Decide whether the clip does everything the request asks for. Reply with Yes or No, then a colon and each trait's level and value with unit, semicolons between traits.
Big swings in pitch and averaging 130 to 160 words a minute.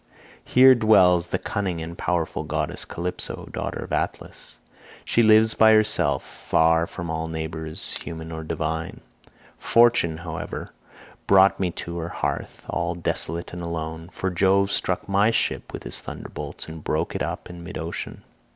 No: average, 3.2 semitones; average, 155 wpm